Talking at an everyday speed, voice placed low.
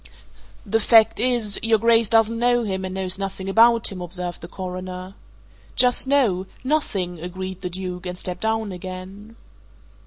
No: average, 155 wpm; high, 195 Hz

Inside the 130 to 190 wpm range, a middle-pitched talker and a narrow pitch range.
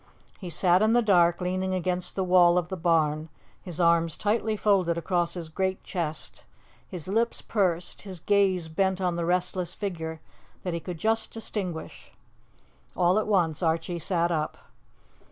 Yes: average, 160 wpm; medium, 180 Hz; narrow, 2.3 semitones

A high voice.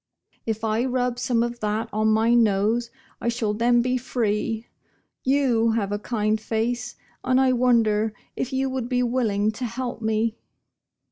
Yes: high, 230 Hz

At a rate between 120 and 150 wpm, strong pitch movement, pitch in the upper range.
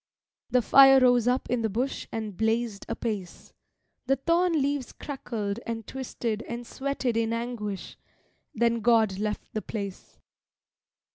No: slow, 135 wpm; average, 2.9 semitones; high, 235 Hz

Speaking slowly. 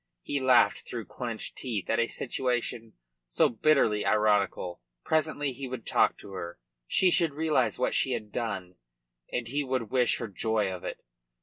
No: average, 170 wpm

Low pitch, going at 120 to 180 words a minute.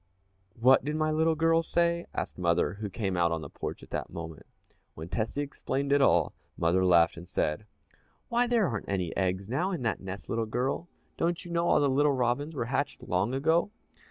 No: low, 130 Hz; fast, 205 wpm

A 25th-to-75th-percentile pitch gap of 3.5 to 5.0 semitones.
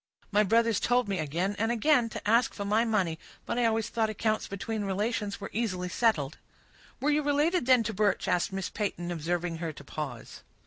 Yes: average, 4.2 semitones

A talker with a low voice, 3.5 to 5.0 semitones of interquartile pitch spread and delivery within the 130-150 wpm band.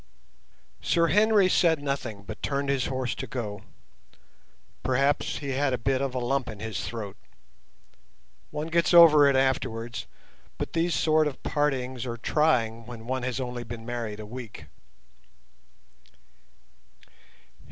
Yes: low, 130 Hz; average, 3.9 semitones; average, 140 wpm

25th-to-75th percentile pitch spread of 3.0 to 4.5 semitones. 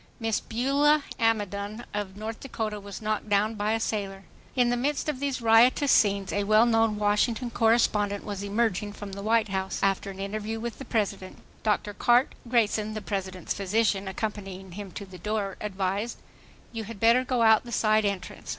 No: narrow, 2.4 semitones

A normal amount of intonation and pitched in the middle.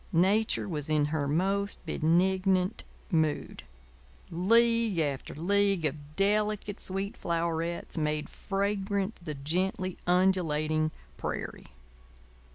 Yes: average, 4.2 semitones; medium, 180 Hz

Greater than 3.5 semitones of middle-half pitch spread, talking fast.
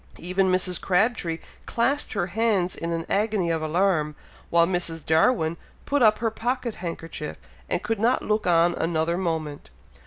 No: average, 4.6 semitones; average, 155 wpm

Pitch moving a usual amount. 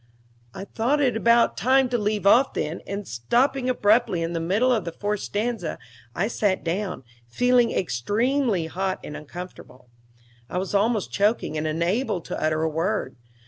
No: wide, 6.0 semitones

